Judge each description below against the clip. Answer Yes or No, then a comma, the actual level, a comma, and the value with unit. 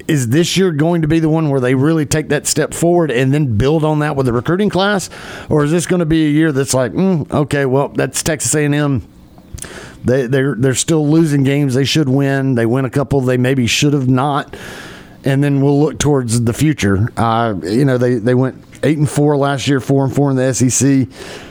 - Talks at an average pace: No, fast, 230 wpm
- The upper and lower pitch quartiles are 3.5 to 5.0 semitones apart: No, average, 3.1 semitones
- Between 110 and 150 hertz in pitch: Yes, medium, 140 Hz